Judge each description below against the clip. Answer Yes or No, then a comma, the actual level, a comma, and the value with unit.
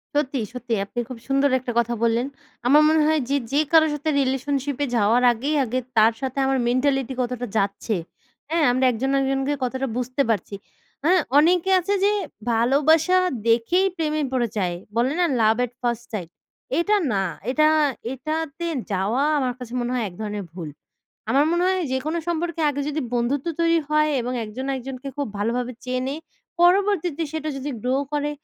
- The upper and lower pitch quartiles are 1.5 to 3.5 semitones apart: No, average, 4.2 semitones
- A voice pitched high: Yes, very high, 265 Hz